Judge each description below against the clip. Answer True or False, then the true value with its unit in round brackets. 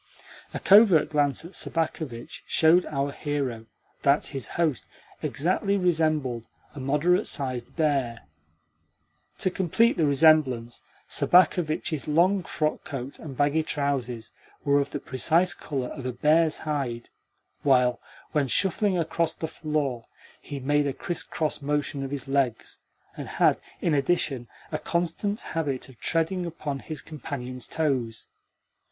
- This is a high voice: False (145 Hz)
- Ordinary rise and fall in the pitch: True (3.5 semitones)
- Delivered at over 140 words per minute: False (135 wpm)